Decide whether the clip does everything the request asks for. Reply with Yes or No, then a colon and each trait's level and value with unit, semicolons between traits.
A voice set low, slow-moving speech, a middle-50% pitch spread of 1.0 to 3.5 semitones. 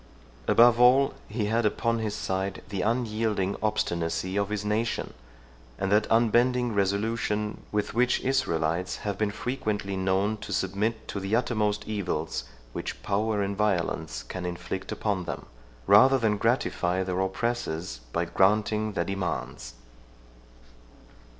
Yes: low, 105 Hz; slow, 130 wpm; average, 2.8 semitones